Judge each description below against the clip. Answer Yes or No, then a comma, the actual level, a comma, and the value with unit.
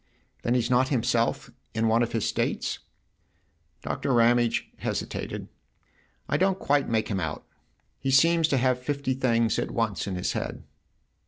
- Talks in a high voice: No, low, 120 Hz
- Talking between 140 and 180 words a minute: Yes, average, 170 wpm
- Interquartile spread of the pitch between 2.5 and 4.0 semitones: Yes, average, 3.2 semitones